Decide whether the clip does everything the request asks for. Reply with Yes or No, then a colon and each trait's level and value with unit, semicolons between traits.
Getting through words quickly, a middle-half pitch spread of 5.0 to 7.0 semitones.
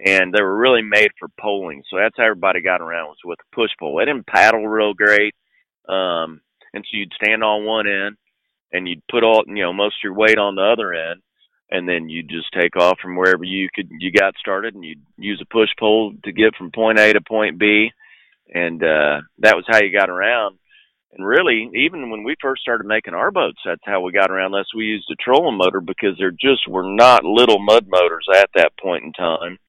No: fast, 230 wpm; average, 2.9 semitones